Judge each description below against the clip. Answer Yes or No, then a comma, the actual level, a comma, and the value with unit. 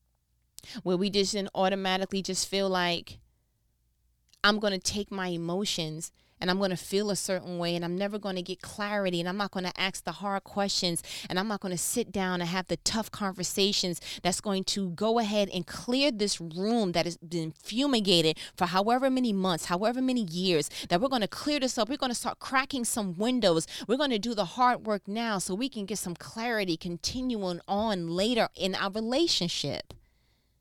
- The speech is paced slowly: No, average, 190 wpm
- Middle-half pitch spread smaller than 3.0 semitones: No, average, 3.5 semitones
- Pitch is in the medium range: No, high, 195 Hz